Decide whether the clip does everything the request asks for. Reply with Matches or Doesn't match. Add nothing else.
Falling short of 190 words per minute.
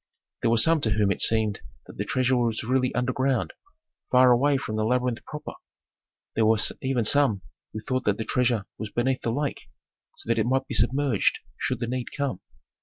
Doesn't match